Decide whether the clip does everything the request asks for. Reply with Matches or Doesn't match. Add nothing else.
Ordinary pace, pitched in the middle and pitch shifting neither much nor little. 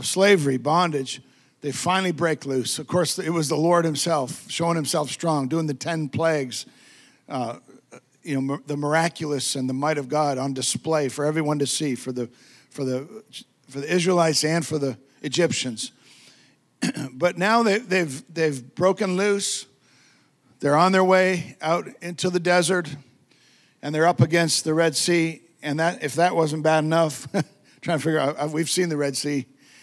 Matches